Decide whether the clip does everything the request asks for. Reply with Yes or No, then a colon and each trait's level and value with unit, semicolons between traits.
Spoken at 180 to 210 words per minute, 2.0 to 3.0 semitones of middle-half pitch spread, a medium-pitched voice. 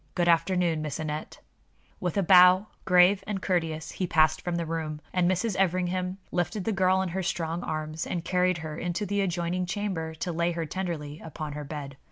Yes: average, 195 wpm; narrow, 2.5 semitones; medium, 175 Hz